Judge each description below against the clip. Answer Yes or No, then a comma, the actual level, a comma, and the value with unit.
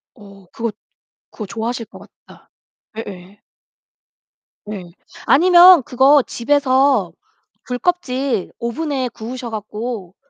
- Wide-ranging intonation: No, average, 4.4 semitones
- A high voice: Yes, high, 240 Hz